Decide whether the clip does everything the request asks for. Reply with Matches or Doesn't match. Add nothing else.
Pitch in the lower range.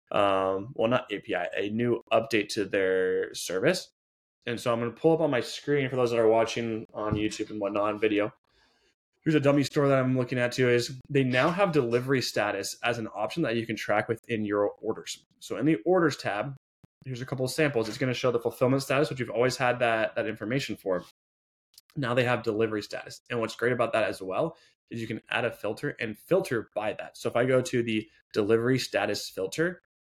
Matches